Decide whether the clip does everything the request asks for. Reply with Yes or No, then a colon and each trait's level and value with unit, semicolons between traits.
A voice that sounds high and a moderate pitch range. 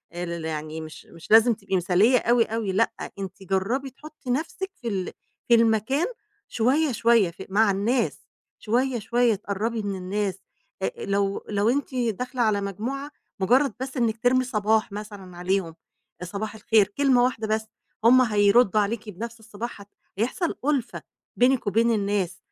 Yes: high, 220 Hz; average, 3.6 semitones